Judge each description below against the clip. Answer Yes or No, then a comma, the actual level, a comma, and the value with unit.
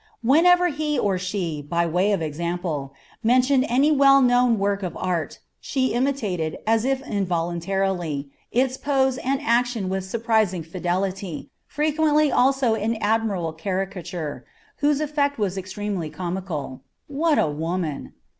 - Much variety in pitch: Yes, wide, 7.0 semitones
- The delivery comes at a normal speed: No, slow, 130 wpm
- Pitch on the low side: No, high, 200 Hz